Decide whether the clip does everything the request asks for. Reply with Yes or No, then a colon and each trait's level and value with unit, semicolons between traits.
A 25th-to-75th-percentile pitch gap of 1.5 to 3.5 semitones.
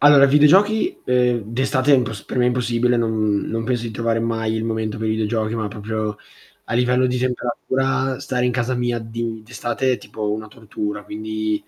Yes: narrow, 2.5 semitones